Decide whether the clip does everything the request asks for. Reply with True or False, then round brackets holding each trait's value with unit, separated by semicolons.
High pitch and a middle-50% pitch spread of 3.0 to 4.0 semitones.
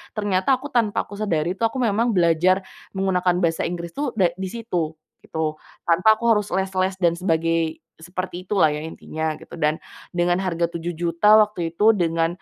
False (180 Hz; 3.7 semitones)